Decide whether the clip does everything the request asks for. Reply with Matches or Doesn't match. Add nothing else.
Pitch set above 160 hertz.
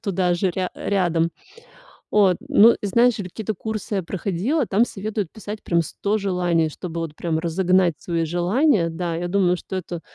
Matches